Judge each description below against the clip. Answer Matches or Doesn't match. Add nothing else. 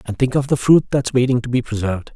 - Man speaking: Matches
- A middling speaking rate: Doesn't match